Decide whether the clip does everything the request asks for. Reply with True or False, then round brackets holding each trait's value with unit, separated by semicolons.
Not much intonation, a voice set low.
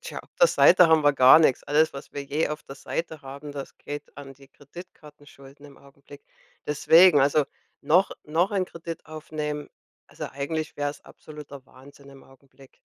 False (2.2 semitones; 145 Hz)